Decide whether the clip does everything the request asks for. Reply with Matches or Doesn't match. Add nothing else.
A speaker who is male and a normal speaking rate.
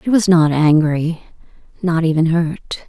Doesn't match